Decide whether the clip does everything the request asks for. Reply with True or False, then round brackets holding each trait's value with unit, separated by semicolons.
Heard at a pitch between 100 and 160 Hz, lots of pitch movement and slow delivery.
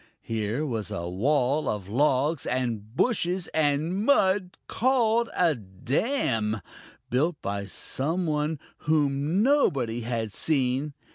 True (140 Hz; 7.1 semitones; 115 wpm)